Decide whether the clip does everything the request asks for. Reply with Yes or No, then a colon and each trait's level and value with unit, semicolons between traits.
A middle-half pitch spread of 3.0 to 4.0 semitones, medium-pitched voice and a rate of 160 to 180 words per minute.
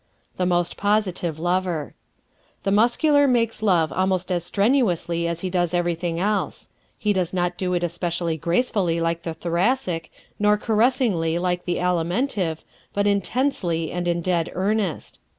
No: average, 3.4 semitones; medium, 180 Hz; average, 150 wpm